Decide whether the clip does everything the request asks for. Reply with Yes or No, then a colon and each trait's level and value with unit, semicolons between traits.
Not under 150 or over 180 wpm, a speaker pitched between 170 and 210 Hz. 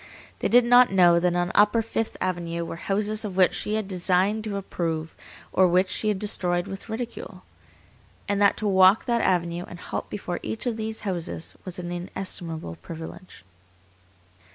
Yes: average, 175 wpm; high, 190 Hz